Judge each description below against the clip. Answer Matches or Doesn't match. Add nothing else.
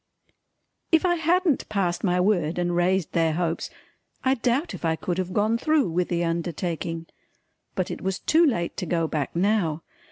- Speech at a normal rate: Matches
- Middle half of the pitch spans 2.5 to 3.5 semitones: Doesn't match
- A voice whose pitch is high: Doesn't match